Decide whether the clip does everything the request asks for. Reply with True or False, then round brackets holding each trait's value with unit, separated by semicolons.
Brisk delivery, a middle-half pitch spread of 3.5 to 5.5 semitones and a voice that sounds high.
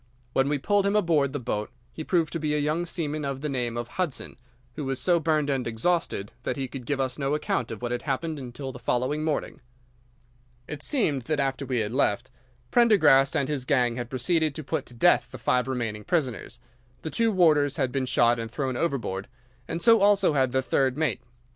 False (215 wpm; 3.9 semitones; 140 Hz)